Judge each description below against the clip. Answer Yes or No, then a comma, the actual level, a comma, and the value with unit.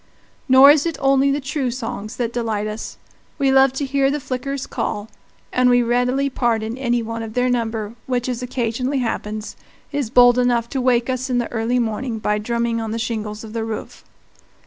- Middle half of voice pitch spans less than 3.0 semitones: Yes, narrow, 2.6 semitones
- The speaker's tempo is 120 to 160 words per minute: No, average, 195 wpm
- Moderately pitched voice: No, high, 245 Hz